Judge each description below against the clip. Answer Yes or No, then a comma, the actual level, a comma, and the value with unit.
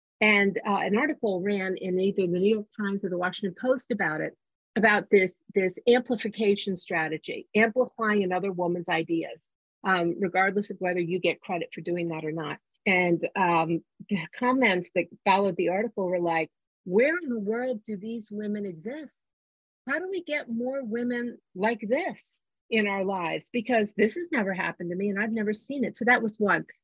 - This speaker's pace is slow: No, average, 185 wpm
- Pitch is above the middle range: Yes, high, 205 Hz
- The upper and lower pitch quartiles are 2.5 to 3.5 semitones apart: No, average, 4.0 semitones